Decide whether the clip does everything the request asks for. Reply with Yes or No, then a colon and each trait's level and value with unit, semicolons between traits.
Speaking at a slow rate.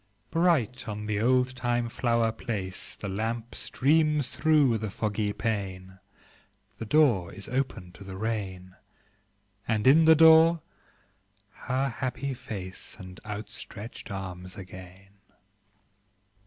Yes: slow, 115 wpm